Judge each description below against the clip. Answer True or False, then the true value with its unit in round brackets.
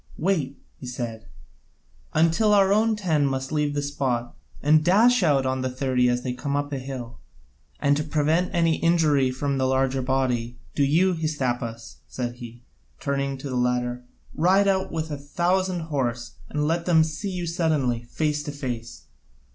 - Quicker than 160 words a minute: True (175 wpm)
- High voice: False (145 Hz)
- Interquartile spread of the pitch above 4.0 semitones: True (4.4 semitones)